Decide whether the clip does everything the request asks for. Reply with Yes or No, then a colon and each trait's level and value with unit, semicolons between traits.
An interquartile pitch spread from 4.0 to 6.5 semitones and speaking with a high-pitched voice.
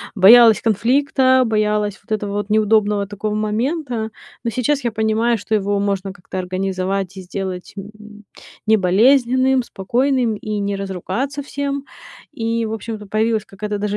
No: average, 3.0 semitones; high, 215 Hz